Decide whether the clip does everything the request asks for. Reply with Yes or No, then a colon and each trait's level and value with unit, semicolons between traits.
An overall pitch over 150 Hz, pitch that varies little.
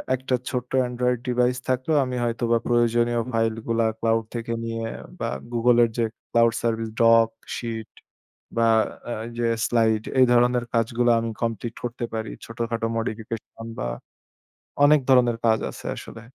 No: low, 115 Hz; narrow, 1.2 semitones